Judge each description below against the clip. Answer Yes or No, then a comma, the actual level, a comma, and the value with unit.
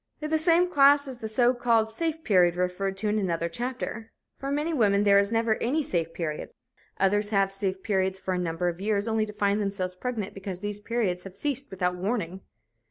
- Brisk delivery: Yes, fast, 210 wpm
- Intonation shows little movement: No, average, 4.2 semitones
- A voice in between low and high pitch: No, high, 205 Hz